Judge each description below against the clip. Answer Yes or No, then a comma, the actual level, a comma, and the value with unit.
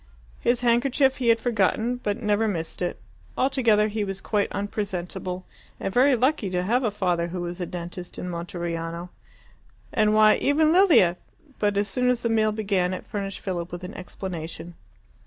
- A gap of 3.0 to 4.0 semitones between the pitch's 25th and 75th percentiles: No, average, 4.6 semitones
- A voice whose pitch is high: Yes, high, 205 Hz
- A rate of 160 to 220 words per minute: Yes, average, 175 wpm